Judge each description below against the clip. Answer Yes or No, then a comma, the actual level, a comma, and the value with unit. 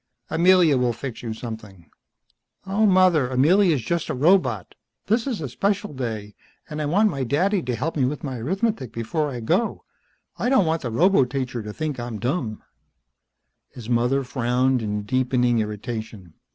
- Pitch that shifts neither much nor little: No, wide, 6.4 semitones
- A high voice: No, low, 130 Hz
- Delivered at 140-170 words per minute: Yes, average, 165 wpm